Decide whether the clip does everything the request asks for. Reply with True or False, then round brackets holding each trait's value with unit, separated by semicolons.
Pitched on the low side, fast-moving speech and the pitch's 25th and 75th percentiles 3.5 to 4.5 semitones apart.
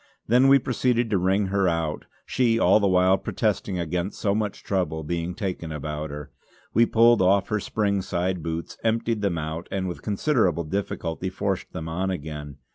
False (95 Hz; 180 wpm; 4.2 semitones)